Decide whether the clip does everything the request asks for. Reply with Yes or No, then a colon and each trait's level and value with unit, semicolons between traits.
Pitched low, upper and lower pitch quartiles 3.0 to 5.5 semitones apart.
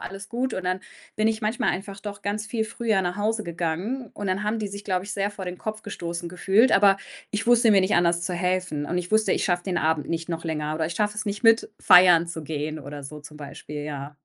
No: medium, 185 Hz; average, 4.0 semitones